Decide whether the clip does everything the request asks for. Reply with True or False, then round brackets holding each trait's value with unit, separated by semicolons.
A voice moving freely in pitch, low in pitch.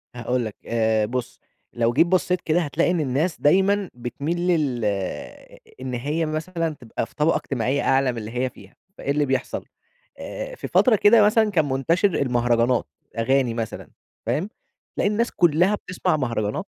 False (6.3 semitones; 145 Hz)